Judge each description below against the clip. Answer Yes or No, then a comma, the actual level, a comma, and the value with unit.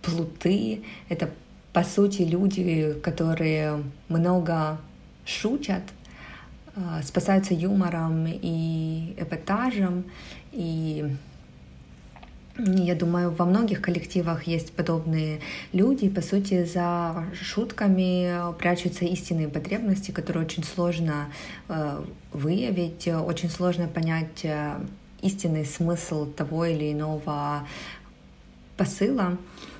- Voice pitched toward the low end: No, medium, 170 Hz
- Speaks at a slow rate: Yes, slow, 85 wpm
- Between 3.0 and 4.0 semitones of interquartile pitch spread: No, narrow, 2.5 semitones